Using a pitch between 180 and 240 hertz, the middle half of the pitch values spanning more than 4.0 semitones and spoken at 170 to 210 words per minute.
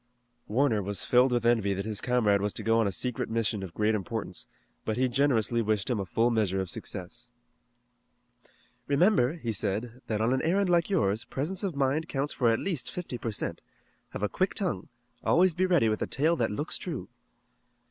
No: low, 120 Hz; average, 5.1 semitones; average, 200 wpm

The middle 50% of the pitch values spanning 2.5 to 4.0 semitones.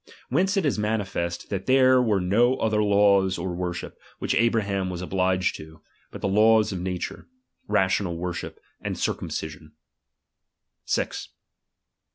Yes: average, 3.5 semitones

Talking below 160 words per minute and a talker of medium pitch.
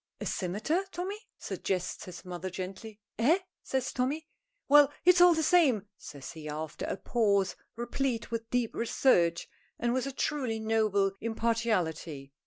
No: average, 145 wpm; high, 225 Hz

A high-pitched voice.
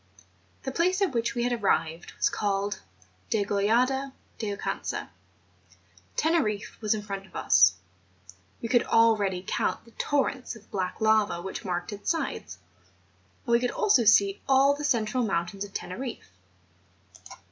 Yes: high, 220 Hz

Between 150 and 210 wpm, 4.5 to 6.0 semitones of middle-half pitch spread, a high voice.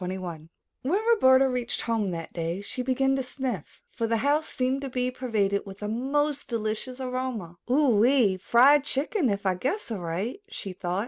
Yes: average, 185 wpm; average, 5.2 semitones; high, 245 Hz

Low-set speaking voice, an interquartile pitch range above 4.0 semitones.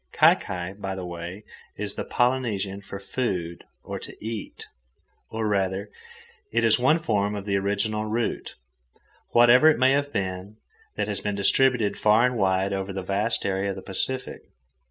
No: low, 105 Hz; average, 3.3 semitones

